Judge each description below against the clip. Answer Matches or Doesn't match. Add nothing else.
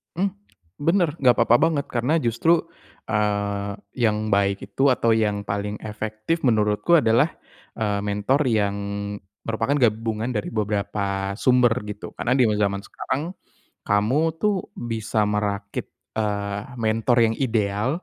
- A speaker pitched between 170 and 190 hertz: Doesn't match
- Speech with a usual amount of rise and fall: Matches